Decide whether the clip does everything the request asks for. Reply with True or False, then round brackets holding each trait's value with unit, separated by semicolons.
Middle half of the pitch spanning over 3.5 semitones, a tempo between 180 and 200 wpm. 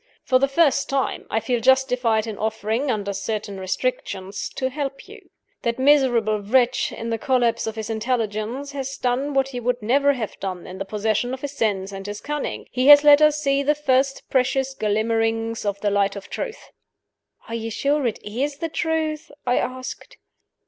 True (4.2 semitones; 185 wpm)